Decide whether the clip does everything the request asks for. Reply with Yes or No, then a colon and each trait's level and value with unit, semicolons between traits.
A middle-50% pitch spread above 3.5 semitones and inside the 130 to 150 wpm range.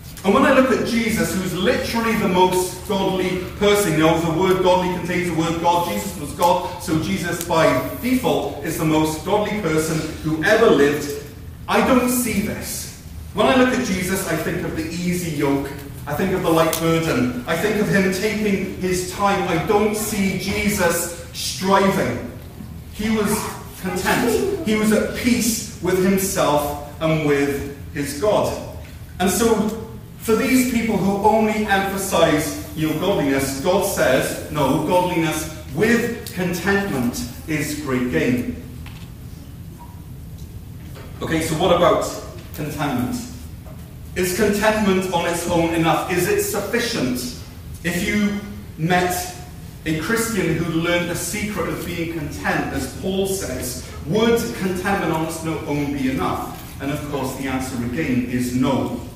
Yes: average, 4.6 semitones; average, 145 wpm